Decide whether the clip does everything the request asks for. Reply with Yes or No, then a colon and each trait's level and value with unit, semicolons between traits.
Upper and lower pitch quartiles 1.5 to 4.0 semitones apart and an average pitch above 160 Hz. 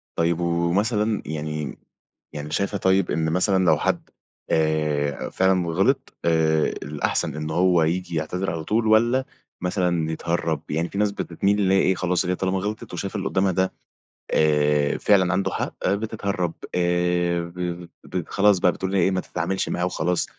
No: average, 3.0 semitones; very low, 90 Hz